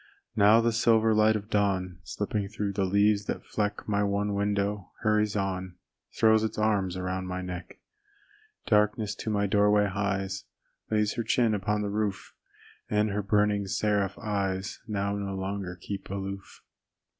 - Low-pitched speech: Yes, low, 100 Hz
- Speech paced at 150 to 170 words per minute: Yes, average, 155 wpm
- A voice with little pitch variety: Yes, narrow, 1.5 semitones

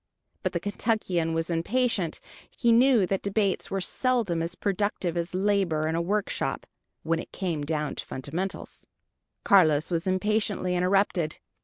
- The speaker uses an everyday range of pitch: Yes, average, 3.7 semitones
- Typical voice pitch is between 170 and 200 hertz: Yes, medium, 185 Hz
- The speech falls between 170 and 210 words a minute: No, average, 145 wpm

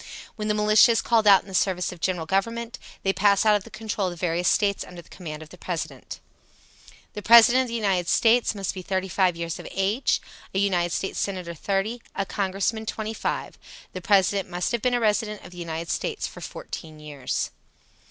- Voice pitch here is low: No, high, 195 Hz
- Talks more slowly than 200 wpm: No, fast, 205 wpm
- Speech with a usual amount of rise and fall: Yes, average, 3.3 semitones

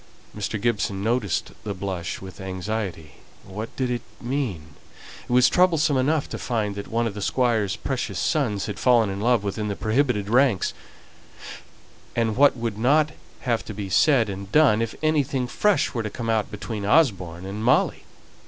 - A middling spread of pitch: Yes, average, 4.1 semitones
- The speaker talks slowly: No, average, 170 wpm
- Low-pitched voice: Yes, low, 110 Hz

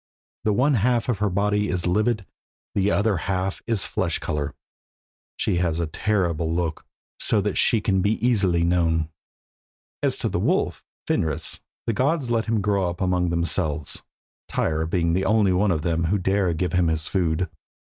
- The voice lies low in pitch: Yes, very low, 95 Hz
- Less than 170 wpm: No, average, 175 wpm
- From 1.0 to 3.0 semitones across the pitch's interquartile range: No, average, 3.6 semitones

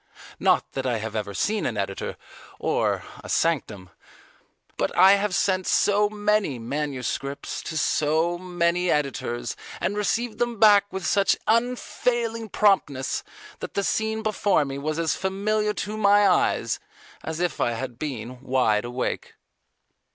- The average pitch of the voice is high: No, medium, 175 Hz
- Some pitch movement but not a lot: No, wide, 7.8 semitones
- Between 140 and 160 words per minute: Yes, average, 145 wpm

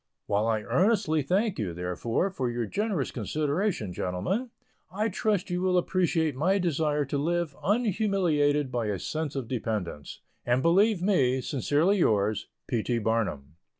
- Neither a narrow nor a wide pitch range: No, wide, 8.3 semitones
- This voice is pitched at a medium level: Yes, medium, 150 Hz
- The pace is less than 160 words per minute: Yes, average, 150 wpm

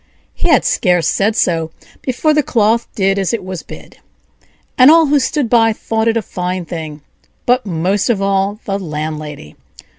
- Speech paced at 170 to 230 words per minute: Yes, average, 175 wpm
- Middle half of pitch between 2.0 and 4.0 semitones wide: No, average, 4.8 semitones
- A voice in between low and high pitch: No, high, 200 Hz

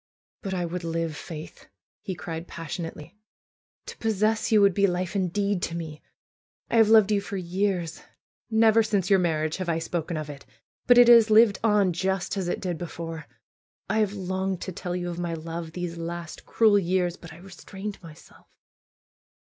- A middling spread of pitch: Yes, average, 3.3 semitones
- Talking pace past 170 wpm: Yes, average, 180 wpm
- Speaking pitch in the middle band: Yes, medium, 180 Hz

